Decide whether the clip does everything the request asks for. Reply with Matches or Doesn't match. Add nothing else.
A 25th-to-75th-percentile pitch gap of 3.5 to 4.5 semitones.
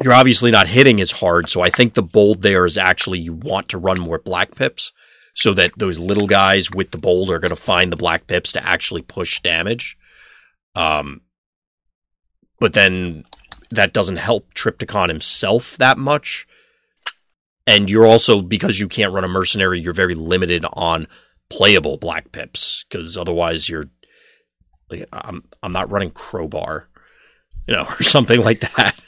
Matches